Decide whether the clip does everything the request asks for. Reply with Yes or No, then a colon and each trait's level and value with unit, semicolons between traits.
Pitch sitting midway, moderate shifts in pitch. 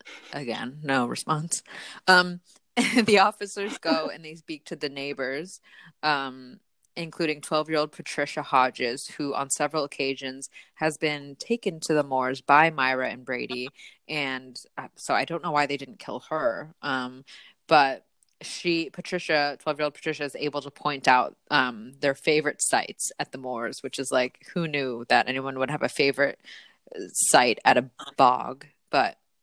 Yes: medium, 145 Hz; average, 3.3 semitones